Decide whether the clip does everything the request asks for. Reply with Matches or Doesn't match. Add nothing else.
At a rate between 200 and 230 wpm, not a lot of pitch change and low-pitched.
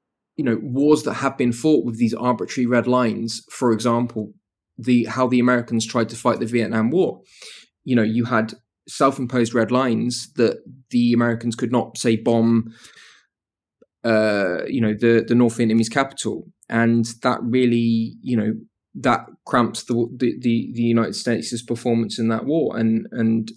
Doesn't match